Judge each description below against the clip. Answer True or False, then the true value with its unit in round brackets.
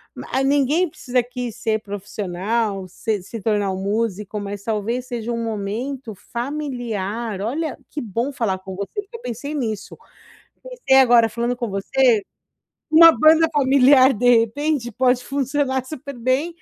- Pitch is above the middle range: True (240 Hz)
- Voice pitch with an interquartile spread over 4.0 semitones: True (4.5 semitones)